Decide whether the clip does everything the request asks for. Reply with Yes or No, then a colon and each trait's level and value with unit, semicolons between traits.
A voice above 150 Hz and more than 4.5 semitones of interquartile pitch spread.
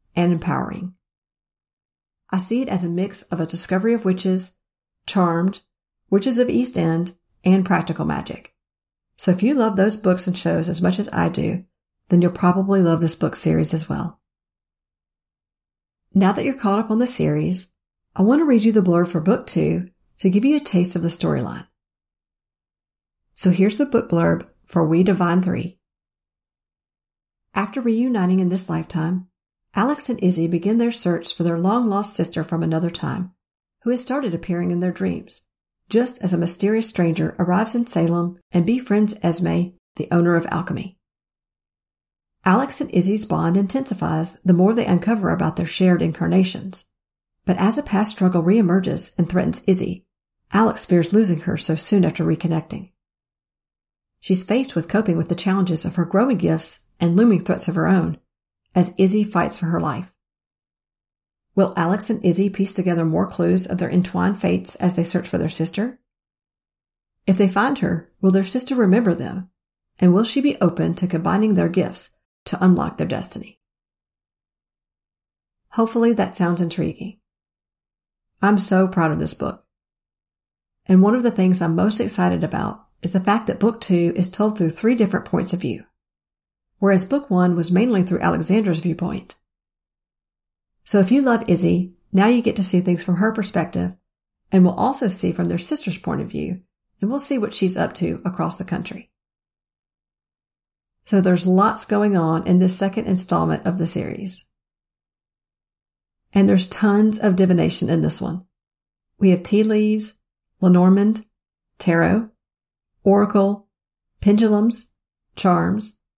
No: medium, 185 Hz; average, 3.3 semitones